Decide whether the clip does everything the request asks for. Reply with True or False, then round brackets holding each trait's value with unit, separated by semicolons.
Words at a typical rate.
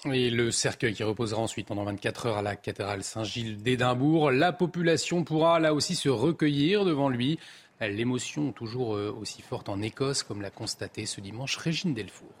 True (175 wpm)